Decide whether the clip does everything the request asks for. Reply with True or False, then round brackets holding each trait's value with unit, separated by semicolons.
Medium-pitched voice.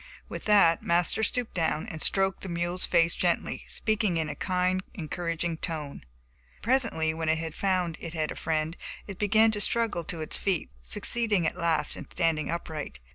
True (170 Hz)